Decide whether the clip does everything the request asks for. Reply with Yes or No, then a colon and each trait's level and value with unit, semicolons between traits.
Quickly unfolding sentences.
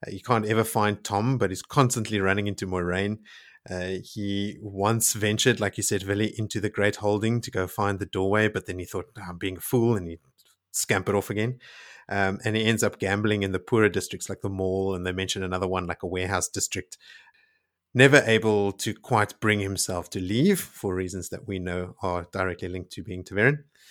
Yes: fast, 210 wpm